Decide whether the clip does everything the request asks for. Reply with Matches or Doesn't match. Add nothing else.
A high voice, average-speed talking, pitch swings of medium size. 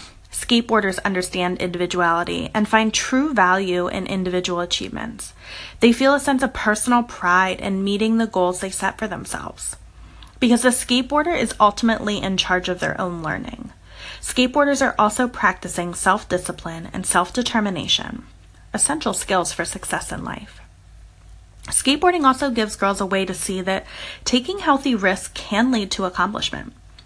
Matches